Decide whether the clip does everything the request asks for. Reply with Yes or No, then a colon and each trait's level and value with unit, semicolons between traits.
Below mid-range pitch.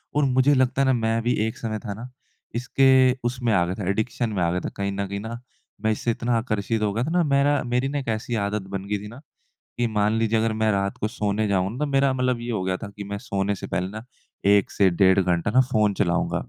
Yes: low, 110 Hz